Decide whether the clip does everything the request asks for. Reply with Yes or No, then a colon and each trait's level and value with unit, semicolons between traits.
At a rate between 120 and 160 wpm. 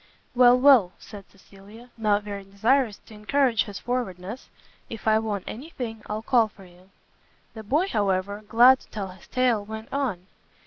No: average, 170 wpm